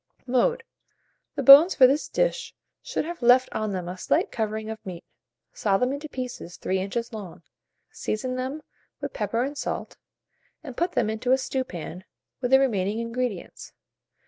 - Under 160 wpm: No, average, 165 wpm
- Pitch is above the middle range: Yes, high, 245 Hz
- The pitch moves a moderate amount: Yes, average, 4.1 semitones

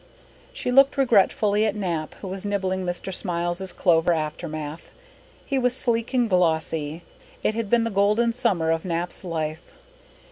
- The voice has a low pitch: No, medium, 185 Hz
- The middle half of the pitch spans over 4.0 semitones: Yes, average, 5.1 semitones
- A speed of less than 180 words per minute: Yes, average, 150 wpm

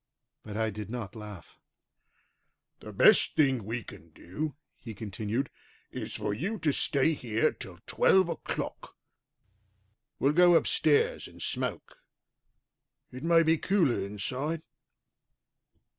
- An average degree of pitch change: No, wide, 7.0 semitones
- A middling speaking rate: No, slow, 120 wpm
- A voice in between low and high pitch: No, low, 125 Hz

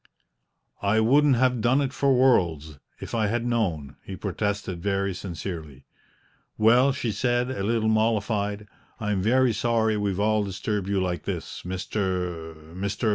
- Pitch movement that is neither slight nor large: Yes, average, 4.1 semitones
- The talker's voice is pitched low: Yes, low, 105 Hz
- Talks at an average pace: Yes, average, 150 wpm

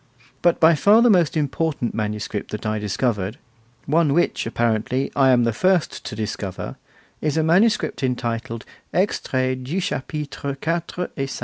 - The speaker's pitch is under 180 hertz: Yes, low, 135 Hz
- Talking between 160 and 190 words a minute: No, average, 150 wpm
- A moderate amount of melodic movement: No, wide, 6.3 semitones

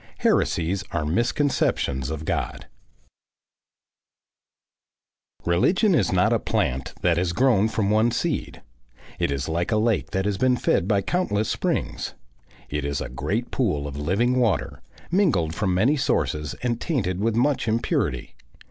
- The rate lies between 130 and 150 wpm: Yes, average, 145 wpm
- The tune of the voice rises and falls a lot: Yes, wide, 6.7 semitones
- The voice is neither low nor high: No, low, 100 Hz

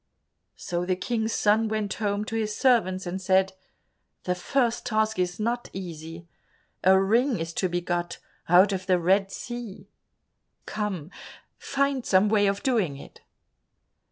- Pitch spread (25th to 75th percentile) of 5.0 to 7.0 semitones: No, average, 3.5 semitones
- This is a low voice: No, high, 195 Hz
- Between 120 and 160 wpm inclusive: Yes, average, 150 wpm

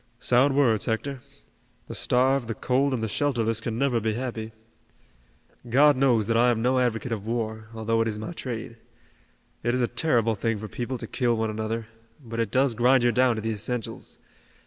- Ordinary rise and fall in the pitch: No, narrow, 2.3 semitones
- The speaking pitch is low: Yes, low, 115 Hz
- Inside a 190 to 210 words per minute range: Yes, average, 195 wpm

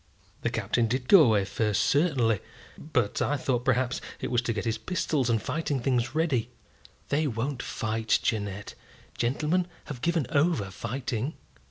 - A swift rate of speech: No, average, 155 wpm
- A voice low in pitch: Yes, low, 125 Hz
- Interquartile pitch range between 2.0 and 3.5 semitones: No, average, 4.5 semitones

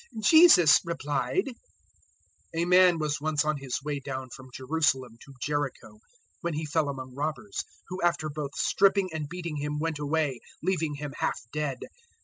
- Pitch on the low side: No, medium, 150 Hz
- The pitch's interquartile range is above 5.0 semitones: No, average, 3.1 semitones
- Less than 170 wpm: Yes, average, 160 wpm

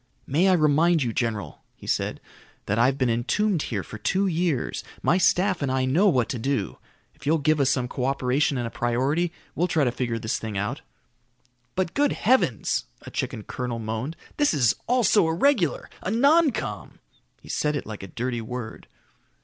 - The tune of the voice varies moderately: No, wide, 6.7 semitones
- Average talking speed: Yes, average, 190 wpm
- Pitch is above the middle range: No, medium, 140 Hz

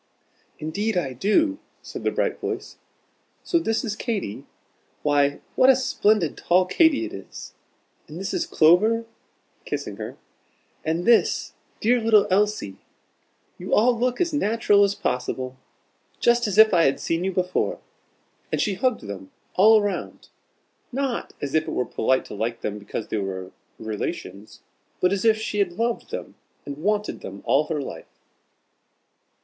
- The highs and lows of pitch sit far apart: Yes, wide, 8.0 semitones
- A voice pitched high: Yes, high, 195 Hz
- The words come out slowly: No, average, 155 wpm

